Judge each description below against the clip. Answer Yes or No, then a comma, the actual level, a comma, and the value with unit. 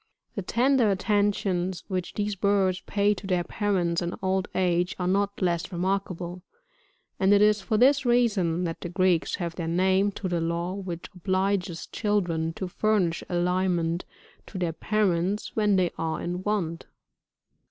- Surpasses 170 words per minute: No, average, 155 wpm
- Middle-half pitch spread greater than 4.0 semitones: No, average, 2.7 semitones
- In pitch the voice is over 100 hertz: Yes, medium, 185 Hz